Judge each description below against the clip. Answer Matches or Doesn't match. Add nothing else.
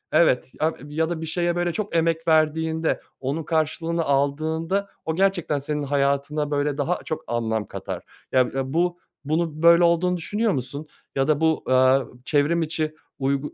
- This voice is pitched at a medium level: Matches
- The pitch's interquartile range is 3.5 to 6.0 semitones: Doesn't match